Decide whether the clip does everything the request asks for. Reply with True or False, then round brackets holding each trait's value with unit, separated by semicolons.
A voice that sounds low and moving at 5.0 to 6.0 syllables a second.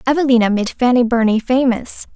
False (240 Hz; 5.6 syllables/s)